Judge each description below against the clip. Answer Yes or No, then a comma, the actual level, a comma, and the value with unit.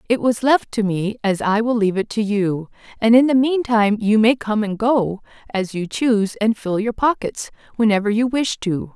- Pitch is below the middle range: No, high, 220 Hz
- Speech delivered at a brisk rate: Yes, fast, 215 wpm